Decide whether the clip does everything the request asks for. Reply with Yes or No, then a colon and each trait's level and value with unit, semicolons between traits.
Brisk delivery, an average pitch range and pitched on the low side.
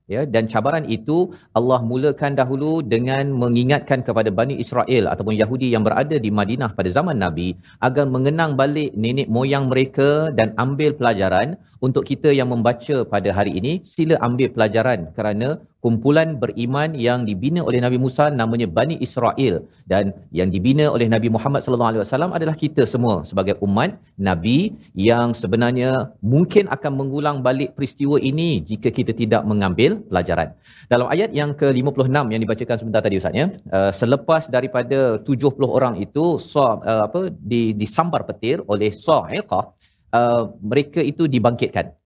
Yes: fast, 155 wpm; average, 4.1 semitones; low, 125 Hz